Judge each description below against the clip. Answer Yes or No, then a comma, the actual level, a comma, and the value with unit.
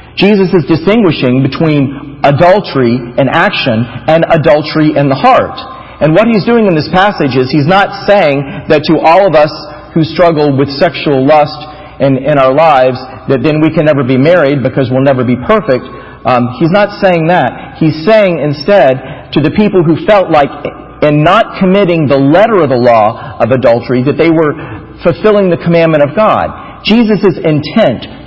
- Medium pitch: Yes, medium, 155 Hz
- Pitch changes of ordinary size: Yes, average, 4.5 semitones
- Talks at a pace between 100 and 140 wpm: No, average, 175 wpm